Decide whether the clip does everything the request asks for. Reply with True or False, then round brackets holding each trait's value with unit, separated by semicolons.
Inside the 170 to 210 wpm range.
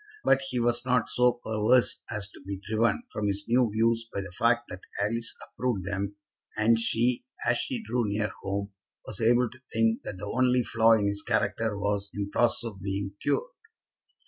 True (190 wpm)